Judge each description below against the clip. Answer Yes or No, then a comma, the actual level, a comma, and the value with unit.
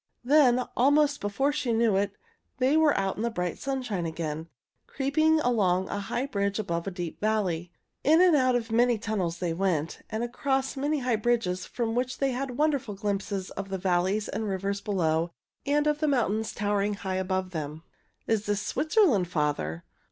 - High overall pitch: Yes, high, 210 Hz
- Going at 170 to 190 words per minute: Yes, average, 180 wpm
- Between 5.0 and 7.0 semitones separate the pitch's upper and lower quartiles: Yes, wide, 5.6 semitones